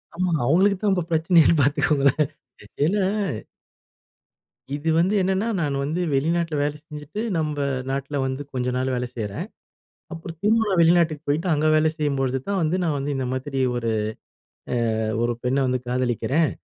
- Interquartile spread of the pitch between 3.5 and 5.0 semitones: Yes, average, 4.1 semitones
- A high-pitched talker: No, medium, 150 Hz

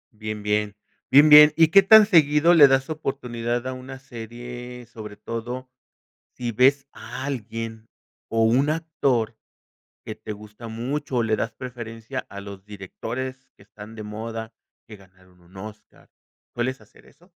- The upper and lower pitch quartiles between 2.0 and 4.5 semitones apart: Yes, average, 3.8 semitones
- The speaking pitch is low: Yes, low, 120 Hz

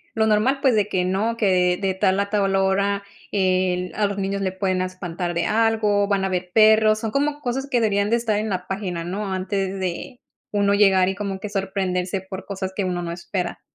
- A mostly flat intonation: Yes, narrow, 2.3 semitones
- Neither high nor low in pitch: No, high, 195 Hz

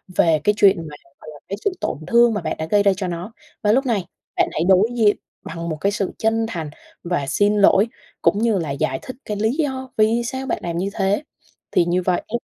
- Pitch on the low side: No, high, 205 Hz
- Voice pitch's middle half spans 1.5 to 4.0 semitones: No, average, 4.6 semitones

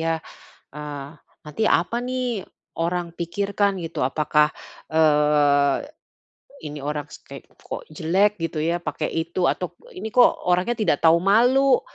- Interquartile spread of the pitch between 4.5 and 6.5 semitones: Yes, average, 5.0 semitones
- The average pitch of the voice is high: No, medium, 170 Hz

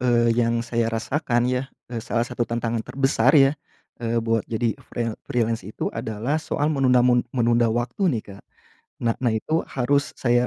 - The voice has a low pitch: Yes, low, 120 Hz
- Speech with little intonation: Yes, narrow, 2.1 semitones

